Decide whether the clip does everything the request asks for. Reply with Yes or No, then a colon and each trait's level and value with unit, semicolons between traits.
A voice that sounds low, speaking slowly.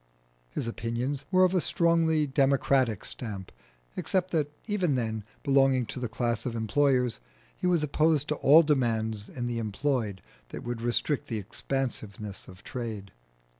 No: low, 125 Hz; average, 150 wpm